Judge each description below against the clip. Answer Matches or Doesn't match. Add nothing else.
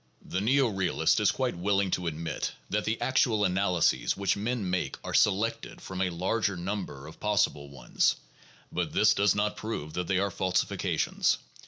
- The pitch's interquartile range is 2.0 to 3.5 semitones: Matches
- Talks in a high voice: Doesn't match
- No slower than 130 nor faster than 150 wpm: Doesn't match